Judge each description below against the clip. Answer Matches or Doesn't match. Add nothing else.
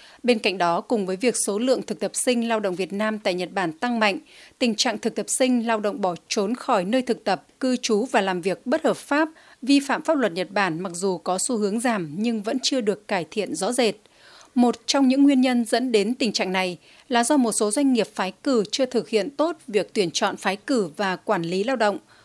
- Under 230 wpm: Doesn't match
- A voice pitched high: Matches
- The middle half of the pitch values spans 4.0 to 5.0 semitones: Matches